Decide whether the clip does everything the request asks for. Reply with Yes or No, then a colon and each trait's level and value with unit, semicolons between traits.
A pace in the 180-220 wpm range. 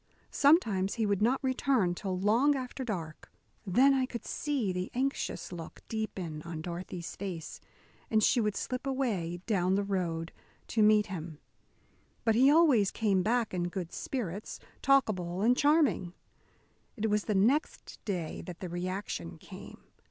No: average, 150 wpm